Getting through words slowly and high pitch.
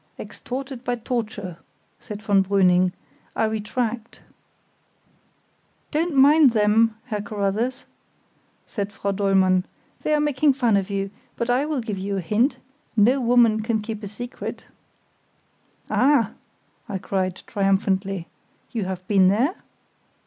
Yes: slow, 125 wpm; high, 215 Hz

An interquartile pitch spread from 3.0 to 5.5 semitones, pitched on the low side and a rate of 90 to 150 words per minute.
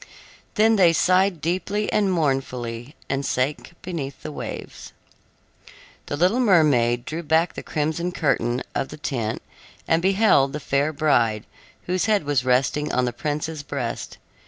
No: average, 5.0 semitones; medium, 150 Hz; average, 145 wpm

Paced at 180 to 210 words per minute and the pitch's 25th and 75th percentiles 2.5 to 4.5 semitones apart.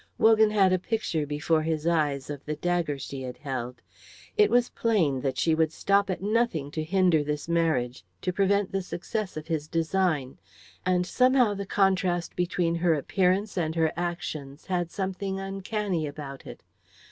No: average, 170 wpm; average, 4.2 semitones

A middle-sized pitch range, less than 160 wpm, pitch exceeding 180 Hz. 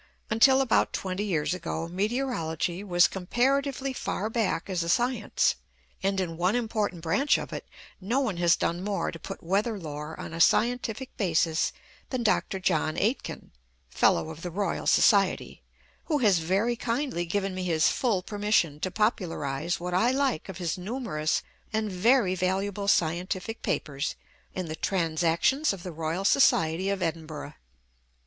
Yes: average, 5.0 semitones; average, 145 wpm; high, 190 Hz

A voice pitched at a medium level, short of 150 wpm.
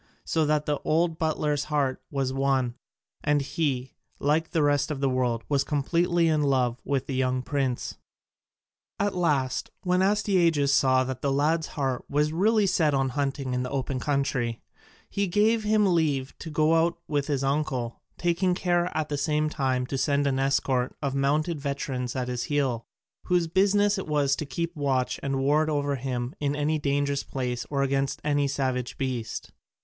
No: medium, 145 Hz; average, 175 wpm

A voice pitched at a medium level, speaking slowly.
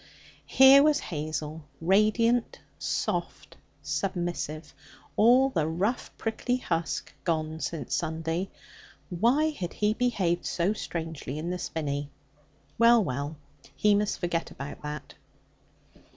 Yes: medium, 175 Hz; slow, 110 wpm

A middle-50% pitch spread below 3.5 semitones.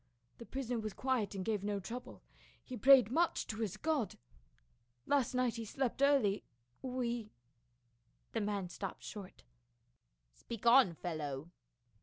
No: average, 4.8 semitones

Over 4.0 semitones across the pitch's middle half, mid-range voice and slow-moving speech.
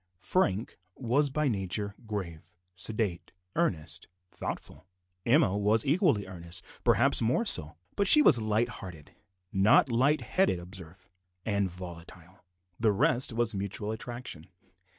No: average, 4.9 semitones; low, 100 Hz; slow, 125 wpm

